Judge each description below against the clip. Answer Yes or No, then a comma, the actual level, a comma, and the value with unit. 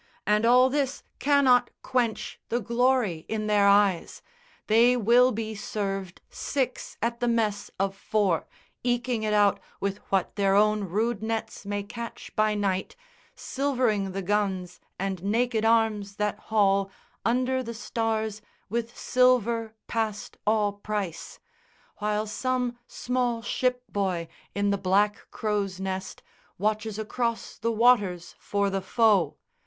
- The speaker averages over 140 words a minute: No, slow, 135 wpm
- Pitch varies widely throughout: No, average, 2.9 semitones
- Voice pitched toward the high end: Yes, high, 215 Hz